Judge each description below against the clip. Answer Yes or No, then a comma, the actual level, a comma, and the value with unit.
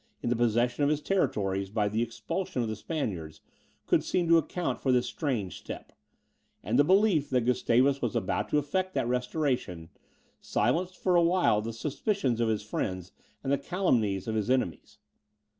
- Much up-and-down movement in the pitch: Yes, wide, 5.9 semitones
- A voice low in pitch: Yes, low, 125 Hz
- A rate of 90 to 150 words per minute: No, average, 175 wpm